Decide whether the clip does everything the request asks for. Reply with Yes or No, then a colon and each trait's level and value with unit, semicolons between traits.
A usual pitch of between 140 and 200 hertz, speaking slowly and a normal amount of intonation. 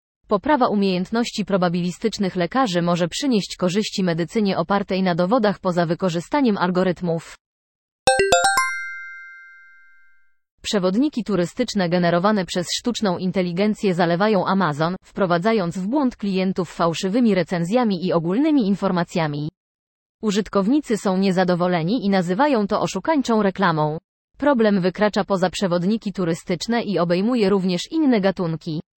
Yes: high, 190 Hz; slow, 100 wpm; average, 3.6 semitones